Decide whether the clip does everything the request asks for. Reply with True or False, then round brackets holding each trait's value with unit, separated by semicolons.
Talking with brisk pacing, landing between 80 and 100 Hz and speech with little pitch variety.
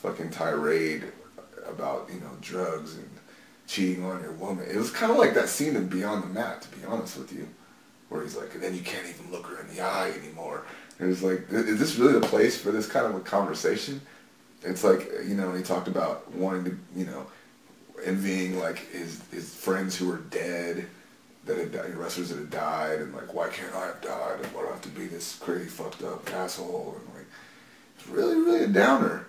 True (220 wpm; 95 Hz; 1.1 semitones)